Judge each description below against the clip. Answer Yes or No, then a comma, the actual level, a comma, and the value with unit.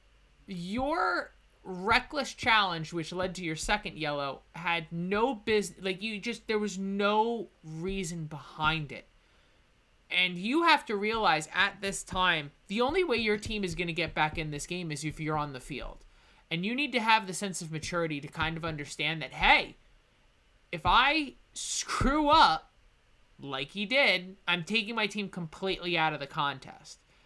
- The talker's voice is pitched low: No, medium, 185 Hz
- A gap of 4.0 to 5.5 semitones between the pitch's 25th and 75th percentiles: Yes, average, 5.2 semitones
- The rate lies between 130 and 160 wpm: No, average, 175 wpm